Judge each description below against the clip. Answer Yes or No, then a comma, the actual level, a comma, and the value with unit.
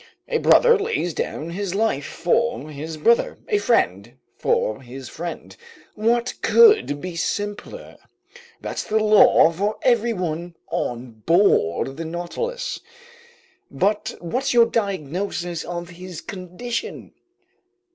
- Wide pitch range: Yes, wide, 6.3 semitones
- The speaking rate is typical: No, slow, 115 wpm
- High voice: No, medium, 180 Hz